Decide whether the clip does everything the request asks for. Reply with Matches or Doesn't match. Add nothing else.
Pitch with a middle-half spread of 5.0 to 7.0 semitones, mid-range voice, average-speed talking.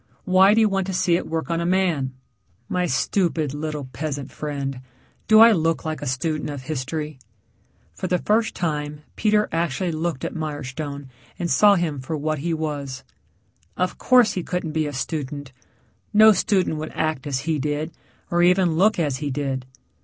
Doesn't match